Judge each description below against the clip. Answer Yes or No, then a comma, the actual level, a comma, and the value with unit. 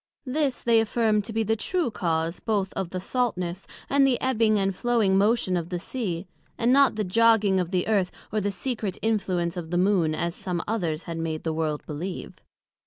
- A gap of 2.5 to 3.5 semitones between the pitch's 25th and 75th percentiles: No, average, 4.4 semitones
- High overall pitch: Yes, high, 195 Hz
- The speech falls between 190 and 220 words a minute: Yes, average, 200 wpm